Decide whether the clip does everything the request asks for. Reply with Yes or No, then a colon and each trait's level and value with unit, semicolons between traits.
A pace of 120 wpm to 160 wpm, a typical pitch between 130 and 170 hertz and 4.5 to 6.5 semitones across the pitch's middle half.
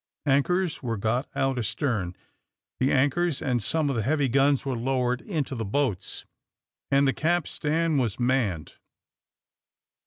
No: slow, 135 wpm; low, 135 Hz; average, 3.2 semitones